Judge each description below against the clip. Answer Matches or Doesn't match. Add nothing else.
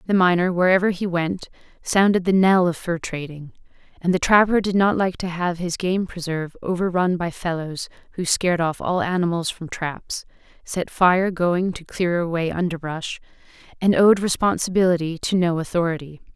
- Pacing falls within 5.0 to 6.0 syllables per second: Matches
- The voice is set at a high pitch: Doesn't match